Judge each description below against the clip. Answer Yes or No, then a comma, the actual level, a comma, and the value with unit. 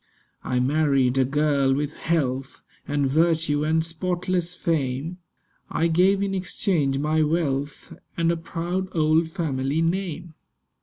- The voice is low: No, medium, 160 Hz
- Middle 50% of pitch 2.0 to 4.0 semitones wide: Yes, average, 3.5 semitones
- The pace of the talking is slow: Yes, slow, 125 wpm